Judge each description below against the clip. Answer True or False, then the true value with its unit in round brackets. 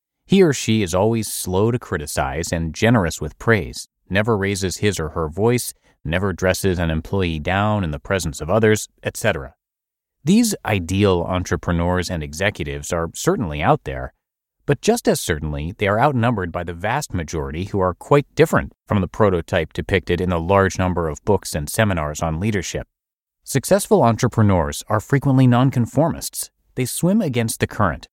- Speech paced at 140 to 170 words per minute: True (165 wpm)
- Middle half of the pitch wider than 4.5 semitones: True (5.2 semitones)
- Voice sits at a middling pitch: False (95 Hz)